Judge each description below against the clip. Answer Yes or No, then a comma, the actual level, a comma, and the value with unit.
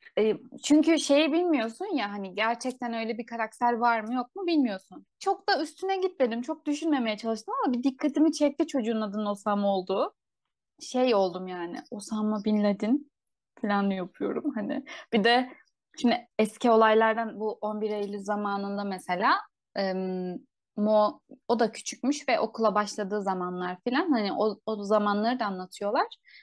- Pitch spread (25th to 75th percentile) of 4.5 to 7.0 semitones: Yes, average, 5.3 semitones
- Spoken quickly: Yes, fast, 145 wpm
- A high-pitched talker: Yes, high, 230 Hz